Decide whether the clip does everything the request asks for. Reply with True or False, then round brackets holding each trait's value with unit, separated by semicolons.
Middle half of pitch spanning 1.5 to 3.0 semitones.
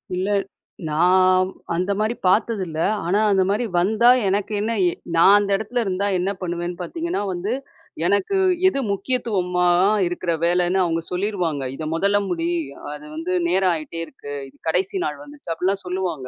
True (2.7 semitones)